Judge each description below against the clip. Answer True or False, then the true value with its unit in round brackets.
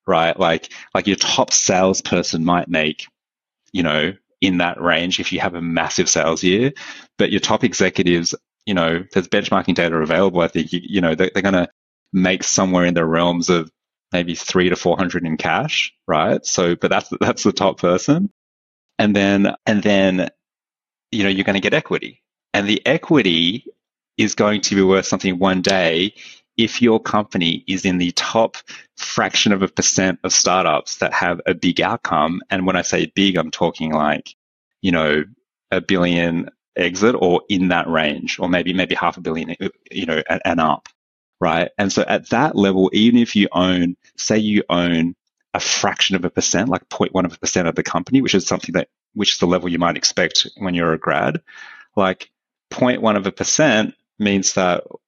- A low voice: True (90 Hz)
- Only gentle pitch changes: True (2.3 semitones)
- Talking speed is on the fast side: False (190 wpm)